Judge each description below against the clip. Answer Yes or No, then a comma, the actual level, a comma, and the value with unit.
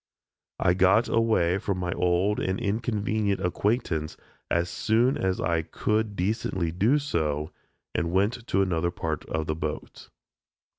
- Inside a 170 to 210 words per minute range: No, average, 140 wpm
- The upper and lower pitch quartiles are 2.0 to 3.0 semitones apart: No, average, 4.2 semitones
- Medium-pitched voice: No, very low, 95 Hz